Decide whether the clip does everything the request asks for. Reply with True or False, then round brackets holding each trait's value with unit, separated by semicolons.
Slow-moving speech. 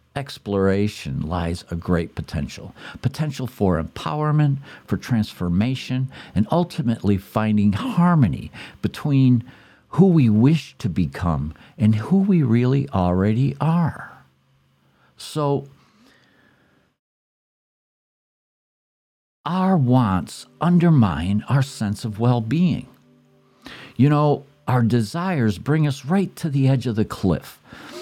True (105 wpm)